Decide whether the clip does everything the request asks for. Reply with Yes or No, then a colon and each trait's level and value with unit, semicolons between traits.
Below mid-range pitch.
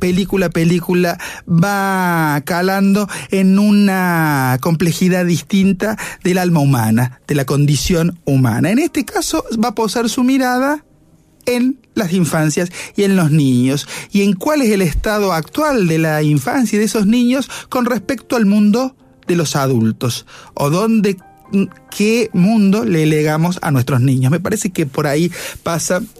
No: medium, 185 Hz